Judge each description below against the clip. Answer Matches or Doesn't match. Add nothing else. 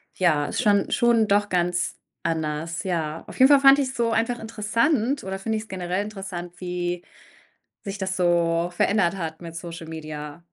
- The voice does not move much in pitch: Doesn't match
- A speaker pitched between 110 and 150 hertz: Doesn't match